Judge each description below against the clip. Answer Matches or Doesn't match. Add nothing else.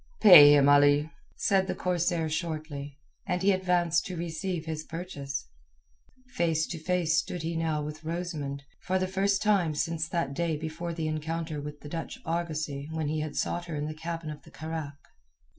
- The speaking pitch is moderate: Matches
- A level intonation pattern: Matches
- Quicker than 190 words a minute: Doesn't match